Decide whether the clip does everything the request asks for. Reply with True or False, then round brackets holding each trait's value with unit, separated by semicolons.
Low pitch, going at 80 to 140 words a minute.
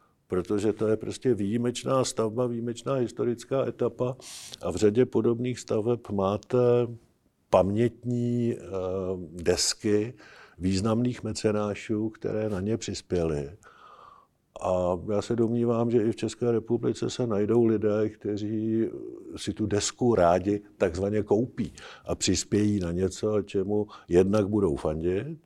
True (110 Hz; 120 wpm)